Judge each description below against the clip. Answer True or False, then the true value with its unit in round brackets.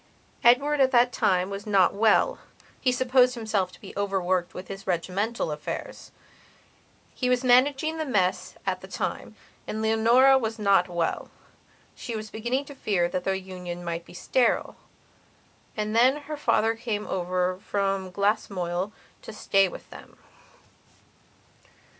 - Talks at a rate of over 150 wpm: False (140 wpm)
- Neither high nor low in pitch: False (210 Hz)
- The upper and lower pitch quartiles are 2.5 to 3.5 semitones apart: False (5.0 semitones)